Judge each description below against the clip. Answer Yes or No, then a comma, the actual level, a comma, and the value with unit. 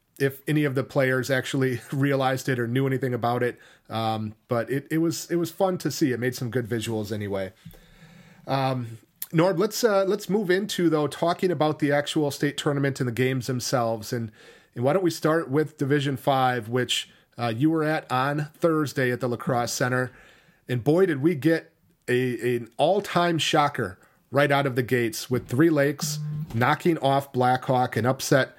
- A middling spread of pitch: Yes, average, 3.9 semitones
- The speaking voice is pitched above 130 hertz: Yes, medium, 140 Hz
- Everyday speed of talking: Yes, average, 190 wpm